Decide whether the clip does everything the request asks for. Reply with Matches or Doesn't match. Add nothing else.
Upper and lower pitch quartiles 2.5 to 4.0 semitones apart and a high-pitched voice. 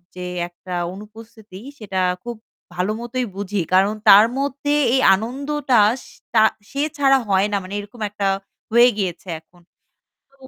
Doesn't match